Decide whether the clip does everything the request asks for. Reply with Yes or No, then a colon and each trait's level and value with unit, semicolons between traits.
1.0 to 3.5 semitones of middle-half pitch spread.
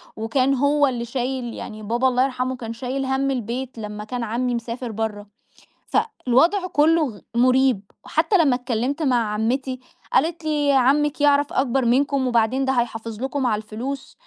Yes: average, 2.8 semitones